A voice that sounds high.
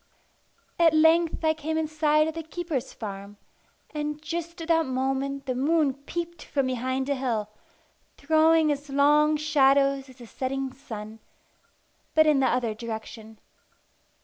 Yes: very high, 280 Hz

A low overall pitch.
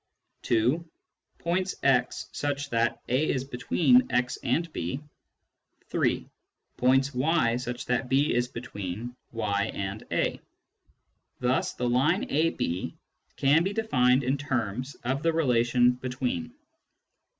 Yes: low, 130 Hz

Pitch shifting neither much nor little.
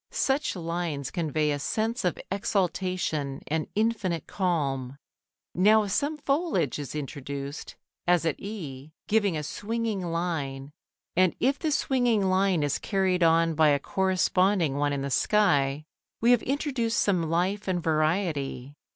No: wide, 5.7 semitones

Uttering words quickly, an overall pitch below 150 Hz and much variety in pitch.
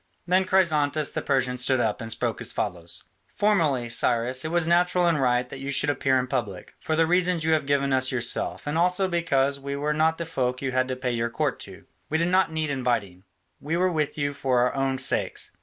No: fast, 225 wpm; medium, 140 Hz; average, 4.4 semitones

